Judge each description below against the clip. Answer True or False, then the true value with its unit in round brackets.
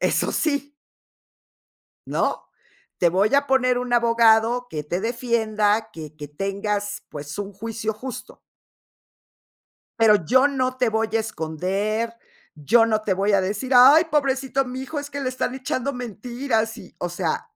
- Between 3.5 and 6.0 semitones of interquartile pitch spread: True (4.1 semitones)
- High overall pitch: True (225 Hz)